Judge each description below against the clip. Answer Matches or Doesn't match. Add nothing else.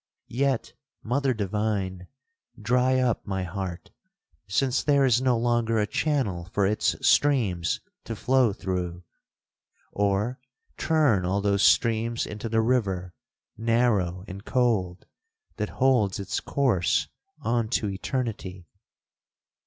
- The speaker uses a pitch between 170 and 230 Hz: Doesn't match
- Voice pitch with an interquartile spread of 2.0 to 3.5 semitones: Doesn't match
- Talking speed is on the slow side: Matches